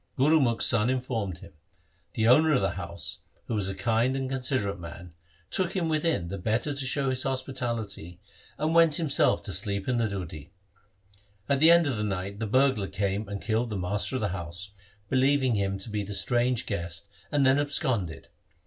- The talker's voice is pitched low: Yes, low, 115 Hz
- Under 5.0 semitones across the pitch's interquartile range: No, average, 5.3 semitones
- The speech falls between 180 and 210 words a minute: Yes, average, 190 wpm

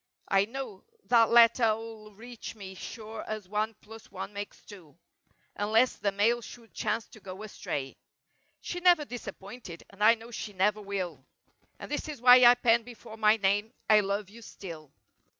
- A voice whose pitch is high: Yes, high, 215 Hz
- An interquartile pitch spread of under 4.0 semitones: Yes, narrow, 2.6 semitones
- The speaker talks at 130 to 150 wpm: No, average, 170 wpm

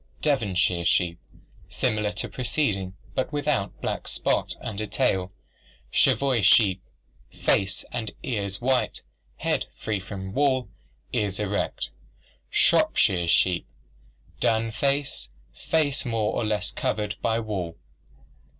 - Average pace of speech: No, slow, 110 wpm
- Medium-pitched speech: No, low, 105 Hz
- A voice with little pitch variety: No, average, 4.7 semitones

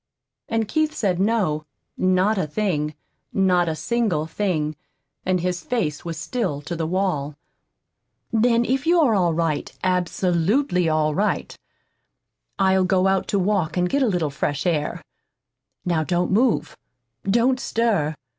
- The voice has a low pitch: No, medium, 185 Hz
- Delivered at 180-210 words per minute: No, average, 140 wpm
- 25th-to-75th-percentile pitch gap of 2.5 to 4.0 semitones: No, average, 5.0 semitones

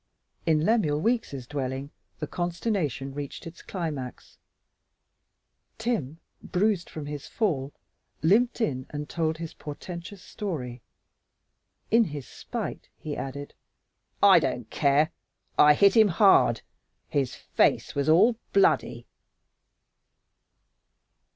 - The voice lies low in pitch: No, medium, 155 Hz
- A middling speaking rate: No, slow, 105 wpm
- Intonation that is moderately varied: No, wide, 5.7 semitones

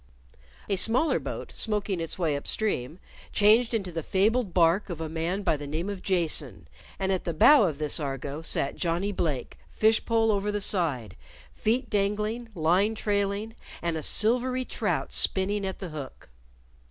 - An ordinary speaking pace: Yes, average, 170 wpm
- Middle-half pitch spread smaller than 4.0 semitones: No, average, 4.7 semitones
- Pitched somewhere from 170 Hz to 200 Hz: Yes, high, 190 Hz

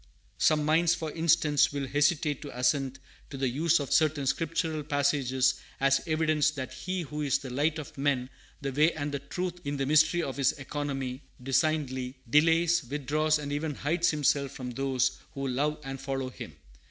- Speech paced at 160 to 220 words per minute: Yes, average, 180 wpm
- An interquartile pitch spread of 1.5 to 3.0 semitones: Yes, narrow, 2.5 semitones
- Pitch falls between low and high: Yes, medium, 145 Hz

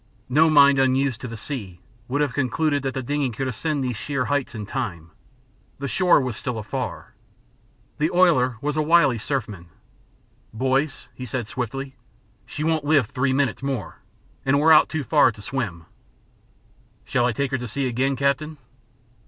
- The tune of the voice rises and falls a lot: No, average, 2.9 semitones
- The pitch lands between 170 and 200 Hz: No, low, 135 Hz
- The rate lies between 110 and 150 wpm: No, average, 170 wpm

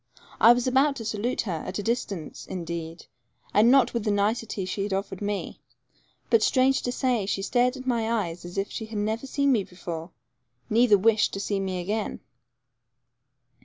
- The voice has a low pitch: No, high, 215 Hz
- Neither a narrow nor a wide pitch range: Yes, average, 4.0 semitones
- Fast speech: No, average, 190 wpm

